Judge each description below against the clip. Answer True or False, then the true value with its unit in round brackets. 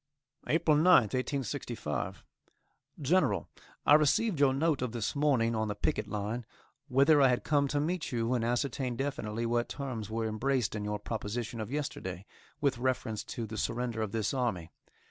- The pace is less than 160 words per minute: False (165 wpm)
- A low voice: True (120 Hz)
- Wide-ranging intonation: False (4.3 semitones)